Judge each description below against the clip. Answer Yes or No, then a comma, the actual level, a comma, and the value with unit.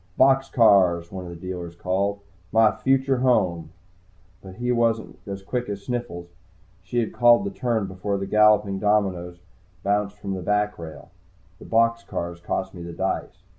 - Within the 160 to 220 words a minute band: Yes, average, 170 wpm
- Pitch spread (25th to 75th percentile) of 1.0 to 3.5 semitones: No, average, 4.2 semitones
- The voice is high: No, low, 100 Hz